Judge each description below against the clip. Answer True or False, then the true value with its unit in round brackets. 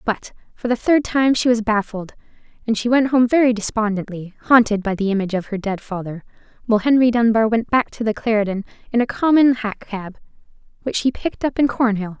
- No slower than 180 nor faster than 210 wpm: True (200 wpm)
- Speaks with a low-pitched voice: False (225 Hz)